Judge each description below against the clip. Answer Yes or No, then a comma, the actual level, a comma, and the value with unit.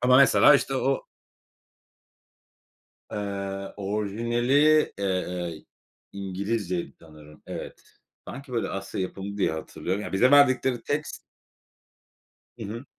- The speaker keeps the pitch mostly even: No, average, 4.7 semitones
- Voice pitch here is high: No, low, 100 Hz